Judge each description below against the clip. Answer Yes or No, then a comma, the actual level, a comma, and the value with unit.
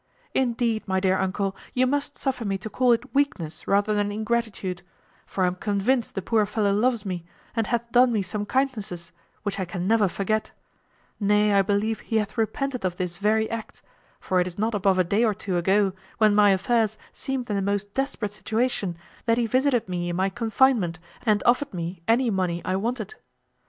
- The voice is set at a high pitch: Yes, high, 210 Hz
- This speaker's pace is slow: No, average, 200 wpm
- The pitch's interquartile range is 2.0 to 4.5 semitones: Yes, average, 3.5 semitones